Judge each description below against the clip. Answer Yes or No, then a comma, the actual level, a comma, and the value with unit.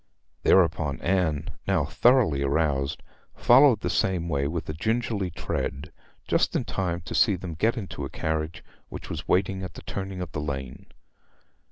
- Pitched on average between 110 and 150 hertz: No, very low, 85 Hz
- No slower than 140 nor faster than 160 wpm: No, average, 170 wpm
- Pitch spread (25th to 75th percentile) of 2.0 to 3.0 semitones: No, average, 4.3 semitones